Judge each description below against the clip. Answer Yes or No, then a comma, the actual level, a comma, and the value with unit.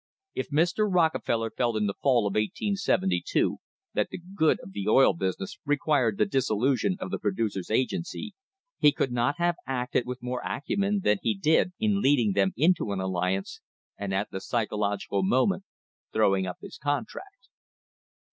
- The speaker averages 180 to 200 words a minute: No, average, 160 wpm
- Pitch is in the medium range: No, low, 125 Hz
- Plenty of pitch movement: Yes, wide, 8.8 semitones